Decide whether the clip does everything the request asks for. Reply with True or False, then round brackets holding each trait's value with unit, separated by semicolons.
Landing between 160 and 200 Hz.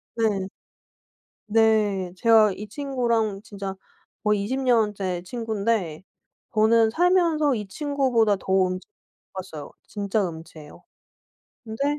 False (215 Hz)